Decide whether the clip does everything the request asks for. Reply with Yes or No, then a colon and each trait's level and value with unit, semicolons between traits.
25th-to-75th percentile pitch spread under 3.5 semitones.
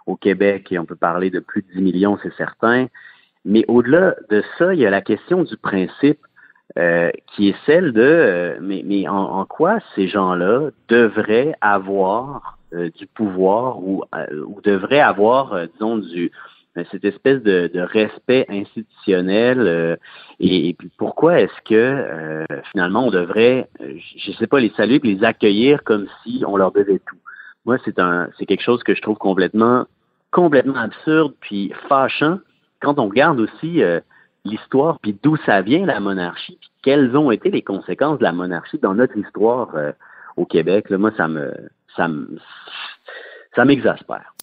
No: average, 4.2 semitones